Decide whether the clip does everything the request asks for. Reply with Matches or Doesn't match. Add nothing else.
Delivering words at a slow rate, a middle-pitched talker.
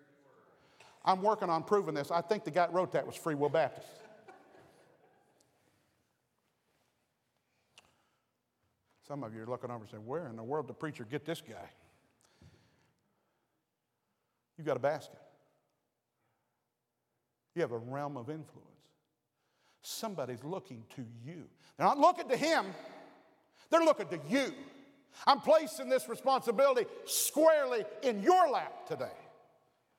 Matches